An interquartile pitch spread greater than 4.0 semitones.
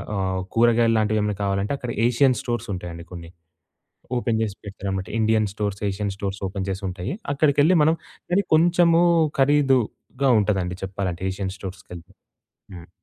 Yes: average, 4.5 semitones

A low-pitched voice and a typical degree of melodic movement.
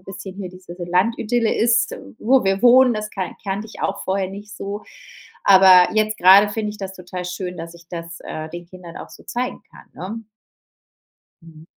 No: high, 195 Hz; average, 3.0 semitones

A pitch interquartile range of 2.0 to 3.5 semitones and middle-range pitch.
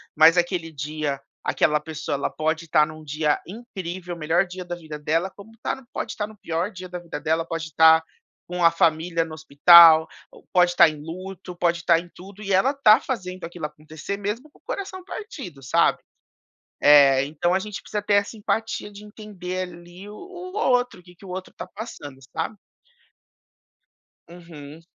No: average, 4.0 semitones; medium, 175 Hz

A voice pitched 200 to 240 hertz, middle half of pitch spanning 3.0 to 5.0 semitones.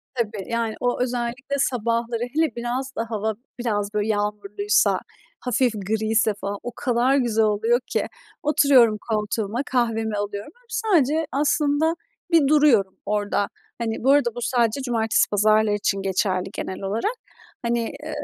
Yes: high, 230 Hz; average, 3.5 semitones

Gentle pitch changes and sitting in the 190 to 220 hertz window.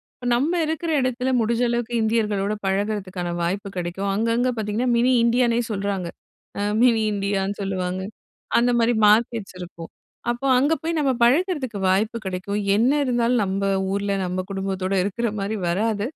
No: average, 3.6 semitones; high, 215 Hz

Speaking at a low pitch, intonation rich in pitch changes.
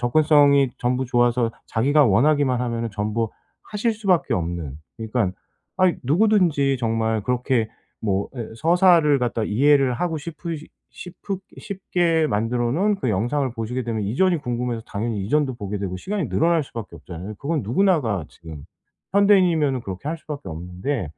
Yes: low, 125 Hz; wide, 6.1 semitones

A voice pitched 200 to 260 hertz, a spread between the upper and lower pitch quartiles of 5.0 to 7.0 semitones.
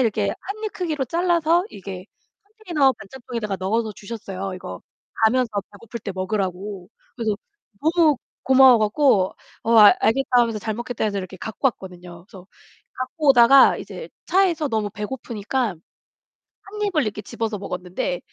Yes: high, 225 Hz; wide, 5.6 semitones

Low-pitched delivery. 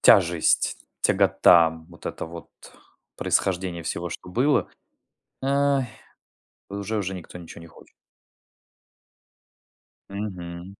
Yes: very low, 90 Hz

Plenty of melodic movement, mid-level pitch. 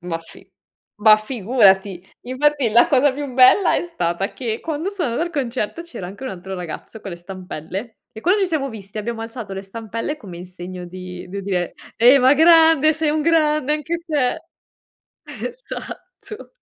No: wide, 7.7 semitones; high, 235 Hz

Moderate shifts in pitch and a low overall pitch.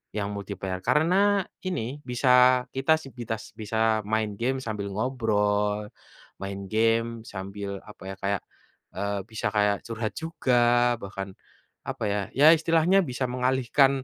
Yes: average, 4.2 semitones; low, 115 Hz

